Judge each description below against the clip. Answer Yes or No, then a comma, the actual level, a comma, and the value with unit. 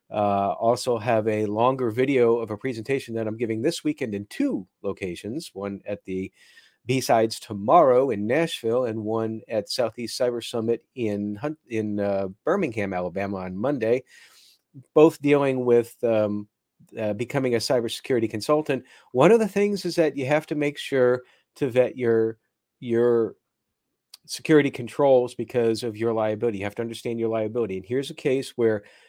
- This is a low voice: Yes, low, 115 Hz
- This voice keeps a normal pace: Yes, average, 160 wpm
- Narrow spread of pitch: No, average, 3.6 semitones